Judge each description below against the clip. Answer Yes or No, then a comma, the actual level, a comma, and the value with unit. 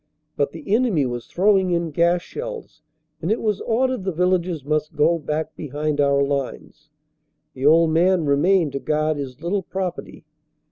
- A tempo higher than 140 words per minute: Yes, average, 160 wpm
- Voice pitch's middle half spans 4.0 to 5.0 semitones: Yes, average, 4.3 semitones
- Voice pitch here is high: No, medium, 165 Hz